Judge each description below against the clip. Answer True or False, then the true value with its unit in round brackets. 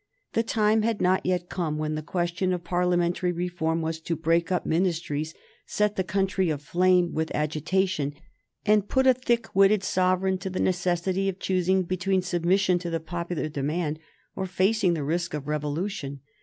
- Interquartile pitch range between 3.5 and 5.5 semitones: False (2.7 semitones)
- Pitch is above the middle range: False (180 Hz)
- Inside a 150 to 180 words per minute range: True (170 wpm)